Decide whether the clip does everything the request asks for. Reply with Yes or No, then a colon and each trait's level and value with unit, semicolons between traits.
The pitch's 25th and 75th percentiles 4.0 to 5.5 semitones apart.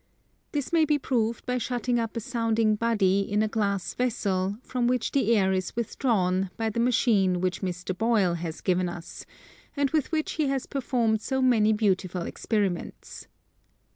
Yes: average, 4.6 semitones